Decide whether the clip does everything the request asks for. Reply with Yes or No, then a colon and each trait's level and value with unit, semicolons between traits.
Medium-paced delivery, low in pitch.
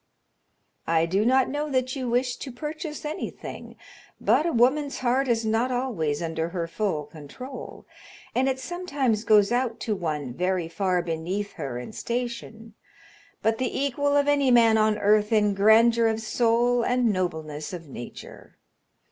No: average, 155 wpm; high, 225 Hz